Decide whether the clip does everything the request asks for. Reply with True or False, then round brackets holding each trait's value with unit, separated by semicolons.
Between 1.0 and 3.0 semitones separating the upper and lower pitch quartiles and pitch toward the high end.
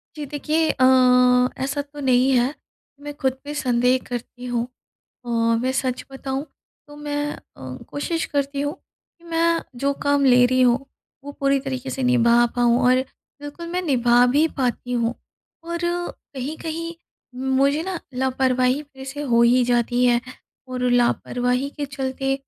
True (2.7 semitones; 265 Hz)